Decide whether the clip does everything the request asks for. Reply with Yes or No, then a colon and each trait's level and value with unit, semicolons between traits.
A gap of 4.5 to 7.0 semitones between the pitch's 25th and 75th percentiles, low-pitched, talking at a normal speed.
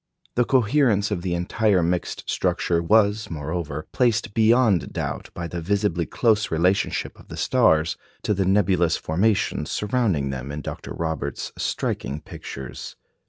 Yes: average, 4.8 semitones; very low, 90 Hz; average, 145 wpm